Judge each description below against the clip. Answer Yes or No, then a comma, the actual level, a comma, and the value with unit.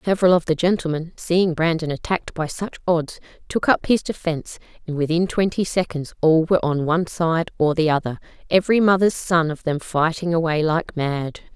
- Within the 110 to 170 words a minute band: No, average, 180 wpm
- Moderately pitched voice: Yes, medium, 165 Hz